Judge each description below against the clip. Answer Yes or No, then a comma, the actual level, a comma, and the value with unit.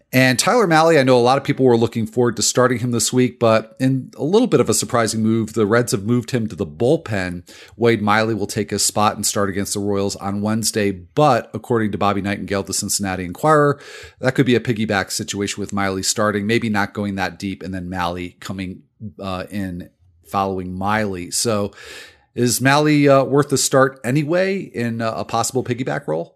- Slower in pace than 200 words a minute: No, fast, 205 wpm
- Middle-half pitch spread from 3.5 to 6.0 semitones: Yes, average, 4.0 semitones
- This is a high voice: No, low, 110 Hz